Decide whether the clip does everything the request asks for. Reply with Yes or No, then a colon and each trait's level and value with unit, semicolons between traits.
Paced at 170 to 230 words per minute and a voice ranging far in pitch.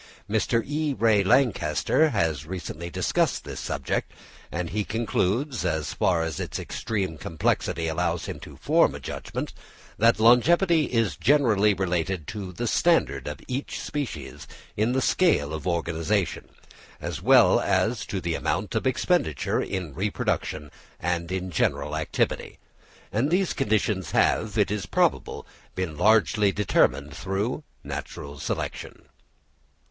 No: slow, 135 wpm; wide, 5.8 semitones